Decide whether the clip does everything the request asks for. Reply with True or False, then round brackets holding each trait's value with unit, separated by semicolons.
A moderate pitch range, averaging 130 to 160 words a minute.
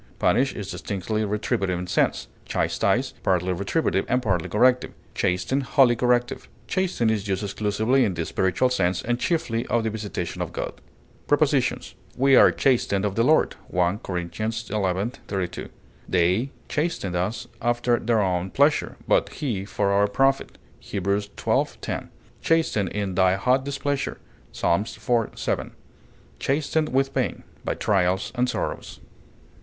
True (4.8 semitones; 145 wpm)